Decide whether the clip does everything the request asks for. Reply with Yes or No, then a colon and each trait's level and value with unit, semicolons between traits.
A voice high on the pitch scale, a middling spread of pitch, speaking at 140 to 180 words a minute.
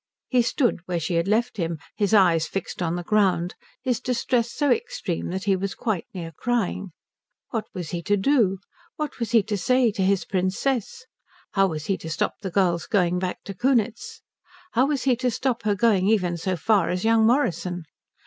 No: high, 200 Hz; average, 4.7 semitones; average, 195 wpm